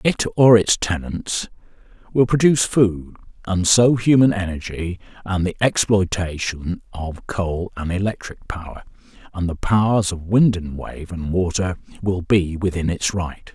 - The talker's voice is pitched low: Yes, very low, 95 Hz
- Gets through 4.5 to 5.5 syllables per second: No, 4.2 syllables/s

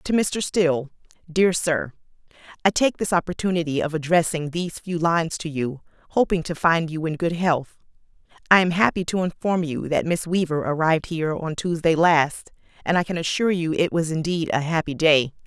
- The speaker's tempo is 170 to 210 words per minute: Yes, average, 180 wpm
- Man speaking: No, female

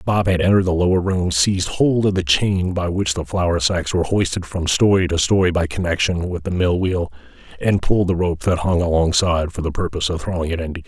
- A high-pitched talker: No, very low, 90 Hz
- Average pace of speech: No, fast, 235 wpm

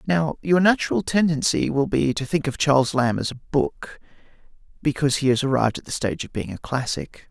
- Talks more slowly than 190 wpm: No, fast, 205 wpm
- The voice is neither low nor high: Yes, medium, 145 Hz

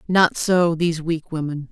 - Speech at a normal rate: Yes, average, 175 wpm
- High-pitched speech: No, medium, 165 Hz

